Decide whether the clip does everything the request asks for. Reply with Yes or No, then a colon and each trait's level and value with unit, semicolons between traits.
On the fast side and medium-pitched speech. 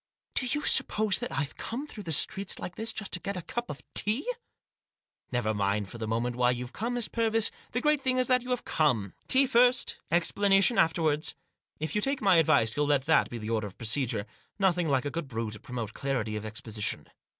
Yes: fast, 230 wpm; medium, 160 Hz